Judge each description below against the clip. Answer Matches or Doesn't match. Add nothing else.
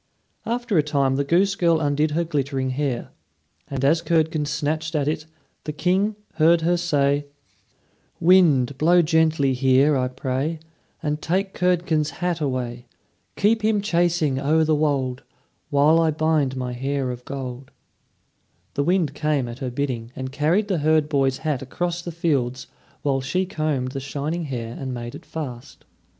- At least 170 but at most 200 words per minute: Doesn't match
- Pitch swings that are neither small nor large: Matches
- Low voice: Doesn't match